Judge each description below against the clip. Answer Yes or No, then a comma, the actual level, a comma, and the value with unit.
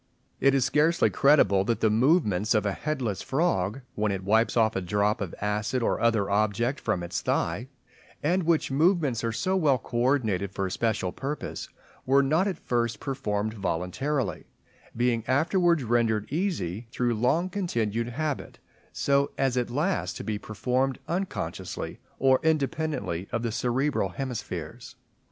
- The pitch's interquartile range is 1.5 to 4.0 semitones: No, wide, 5.4 semitones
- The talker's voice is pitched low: Yes, low, 120 Hz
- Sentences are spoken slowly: No, average, 150 wpm